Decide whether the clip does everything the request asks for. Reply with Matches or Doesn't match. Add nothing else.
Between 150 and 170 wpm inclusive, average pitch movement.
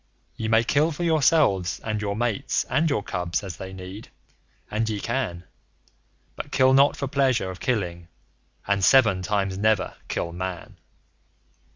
Doesn't match